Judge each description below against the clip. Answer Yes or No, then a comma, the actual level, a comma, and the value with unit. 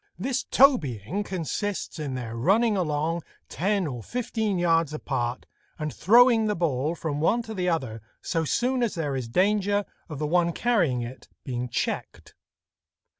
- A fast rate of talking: No, average, 155 wpm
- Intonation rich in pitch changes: Yes, wide, 6.8 semitones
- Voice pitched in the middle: Yes, medium, 170 Hz